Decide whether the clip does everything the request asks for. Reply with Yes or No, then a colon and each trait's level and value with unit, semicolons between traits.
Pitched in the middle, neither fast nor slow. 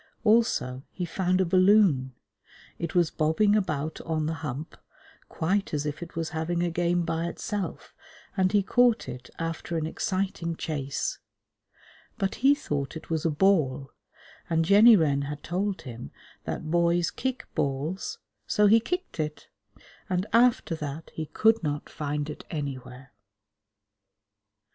Yes: medium, 165 Hz; average, 145 wpm